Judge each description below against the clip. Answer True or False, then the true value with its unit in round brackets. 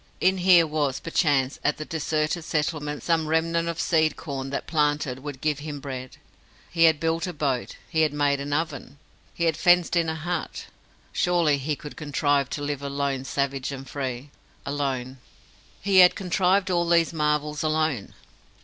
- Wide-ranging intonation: False (2.8 semitones)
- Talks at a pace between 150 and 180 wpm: True (170 wpm)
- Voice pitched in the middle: True (150 Hz)